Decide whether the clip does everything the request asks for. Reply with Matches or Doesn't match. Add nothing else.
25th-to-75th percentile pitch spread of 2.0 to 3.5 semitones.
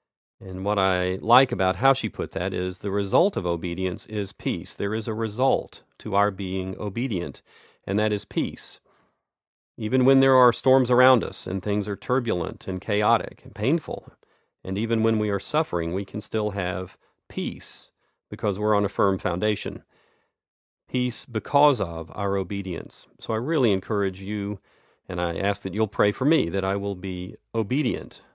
Matches